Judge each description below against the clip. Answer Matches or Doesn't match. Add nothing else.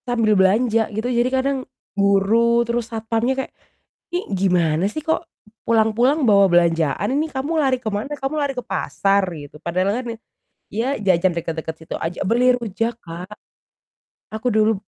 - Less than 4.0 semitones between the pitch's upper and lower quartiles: Doesn't match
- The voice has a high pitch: Matches